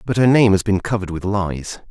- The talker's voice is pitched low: Yes, low, 100 Hz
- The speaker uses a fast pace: Yes, fast, 250 wpm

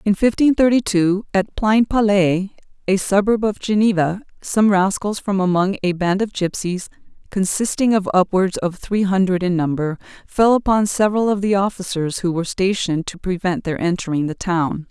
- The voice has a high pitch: Yes, high, 195 Hz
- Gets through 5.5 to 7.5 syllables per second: No, 5.0 syllables/s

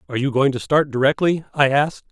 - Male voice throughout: Yes, male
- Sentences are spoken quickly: Yes, fast, 225 wpm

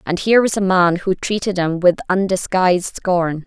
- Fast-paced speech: No, average, 190 wpm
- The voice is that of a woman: Yes, female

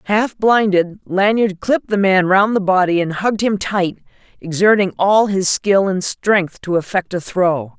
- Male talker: No, female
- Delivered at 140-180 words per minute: Yes, average, 175 wpm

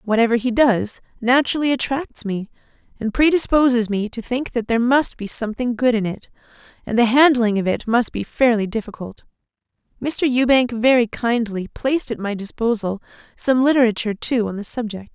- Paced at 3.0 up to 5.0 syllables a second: No, 5.4 syllables/s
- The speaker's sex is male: No, female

